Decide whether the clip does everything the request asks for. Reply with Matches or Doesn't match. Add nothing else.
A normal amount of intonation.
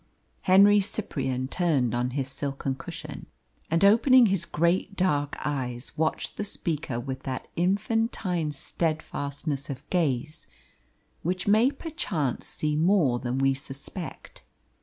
Doesn't match